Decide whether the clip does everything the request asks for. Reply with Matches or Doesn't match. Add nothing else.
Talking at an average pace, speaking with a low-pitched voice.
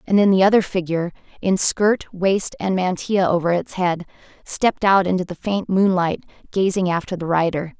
Doesn't match